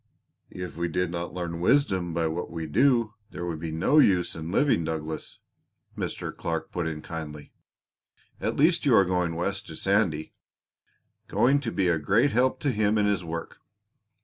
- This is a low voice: Yes, very low, 90 Hz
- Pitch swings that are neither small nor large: Yes, average, 4.6 semitones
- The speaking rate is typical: Yes, average, 175 wpm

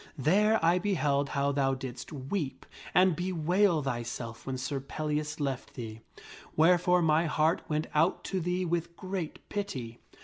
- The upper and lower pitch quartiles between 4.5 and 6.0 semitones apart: Yes, average, 4.8 semitones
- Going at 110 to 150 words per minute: Yes, average, 145 wpm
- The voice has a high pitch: No, medium, 155 Hz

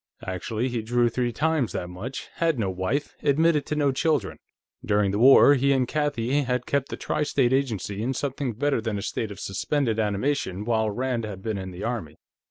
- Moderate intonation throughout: Yes, average, 5.0 semitones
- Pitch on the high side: No, low, 120 Hz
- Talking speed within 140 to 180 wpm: No, average, 200 wpm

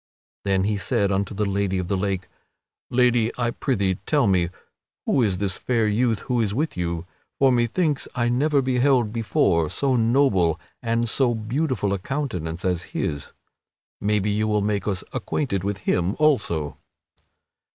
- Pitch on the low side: Yes, low, 105 Hz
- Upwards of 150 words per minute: Yes, average, 160 wpm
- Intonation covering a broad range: No, average, 4.5 semitones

